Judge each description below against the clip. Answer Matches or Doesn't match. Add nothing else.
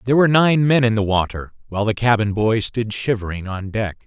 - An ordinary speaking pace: Doesn't match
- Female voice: Doesn't match